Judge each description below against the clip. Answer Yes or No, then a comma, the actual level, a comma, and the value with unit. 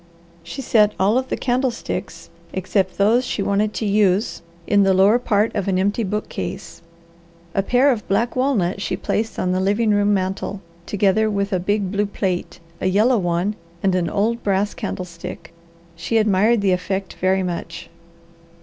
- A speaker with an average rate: Yes, average, 170 wpm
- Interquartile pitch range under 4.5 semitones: Yes, narrow, 2.5 semitones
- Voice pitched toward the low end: No, high, 200 Hz